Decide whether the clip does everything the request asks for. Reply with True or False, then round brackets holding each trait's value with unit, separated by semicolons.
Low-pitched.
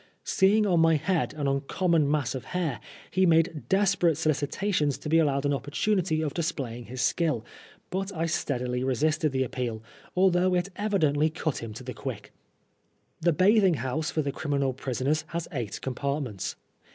False (155 Hz)